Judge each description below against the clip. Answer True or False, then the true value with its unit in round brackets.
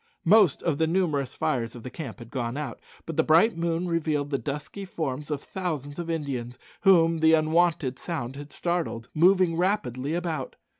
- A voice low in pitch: False (155 Hz)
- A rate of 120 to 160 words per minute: False (180 wpm)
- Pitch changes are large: False (3.7 semitones)